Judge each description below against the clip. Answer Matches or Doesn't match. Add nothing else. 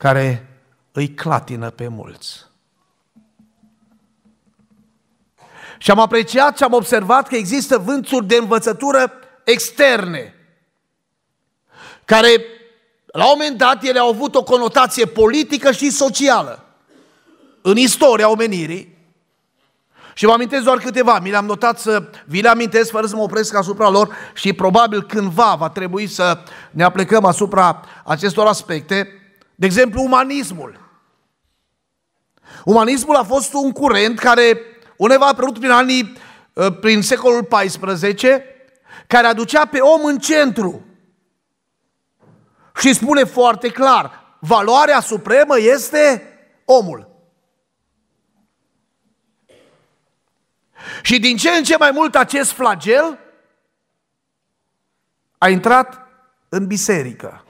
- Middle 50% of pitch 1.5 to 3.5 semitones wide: Doesn't match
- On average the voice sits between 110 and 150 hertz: Doesn't match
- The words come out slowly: Matches